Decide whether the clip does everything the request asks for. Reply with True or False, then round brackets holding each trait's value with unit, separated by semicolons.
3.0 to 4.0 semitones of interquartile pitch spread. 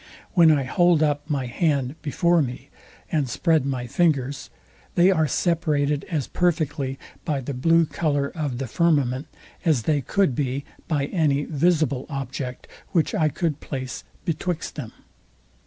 True (3.4 semitones)